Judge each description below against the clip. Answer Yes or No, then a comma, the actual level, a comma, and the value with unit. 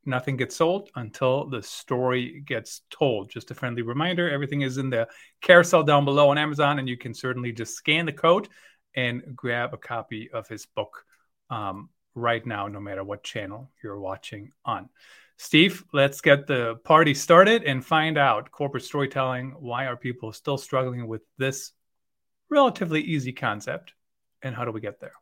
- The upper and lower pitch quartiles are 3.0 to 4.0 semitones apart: Yes, average, 3.5 semitones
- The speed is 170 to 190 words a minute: Yes, average, 175 wpm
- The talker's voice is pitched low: Yes, low, 130 Hz